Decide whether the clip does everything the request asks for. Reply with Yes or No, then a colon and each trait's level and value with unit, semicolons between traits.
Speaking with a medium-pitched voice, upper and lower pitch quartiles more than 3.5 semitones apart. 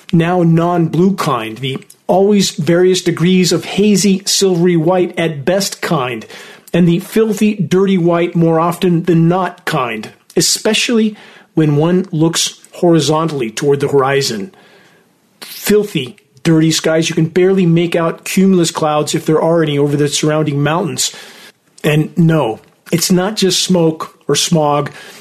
No: medium, 170 Hz; average, 2.9 semitones